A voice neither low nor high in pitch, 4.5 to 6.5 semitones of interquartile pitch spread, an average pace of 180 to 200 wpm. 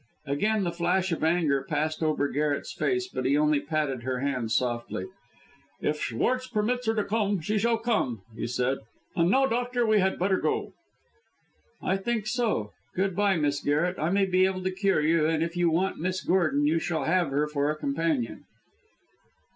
Yes: medium, 170 Hz; average, 5.3 semitones; average, 185 wpm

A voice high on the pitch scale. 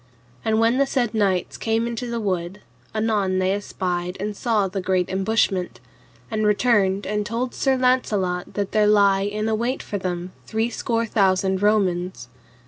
Yes: high, 205 Hz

